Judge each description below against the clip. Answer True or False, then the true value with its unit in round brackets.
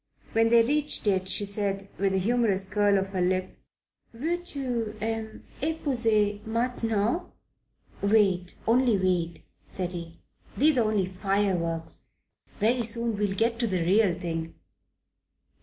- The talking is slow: True (130 wpm)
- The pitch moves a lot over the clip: False (3.6 semitones)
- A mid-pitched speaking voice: False (210 Hz)